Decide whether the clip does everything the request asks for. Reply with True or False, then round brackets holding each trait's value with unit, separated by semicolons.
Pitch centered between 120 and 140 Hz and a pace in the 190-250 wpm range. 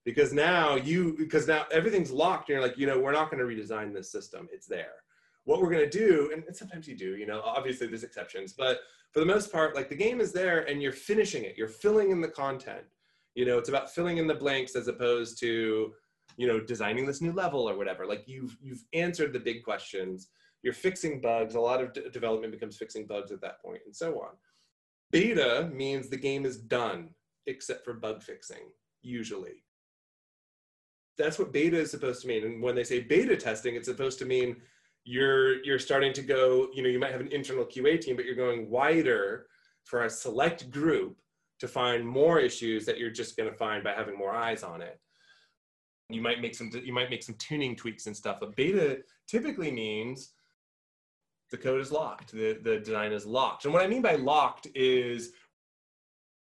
True (135 Hz; 205 wpm)